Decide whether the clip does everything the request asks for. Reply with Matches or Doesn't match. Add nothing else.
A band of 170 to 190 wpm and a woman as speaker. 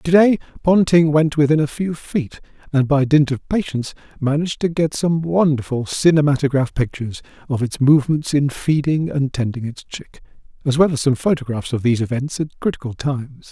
Doesn't match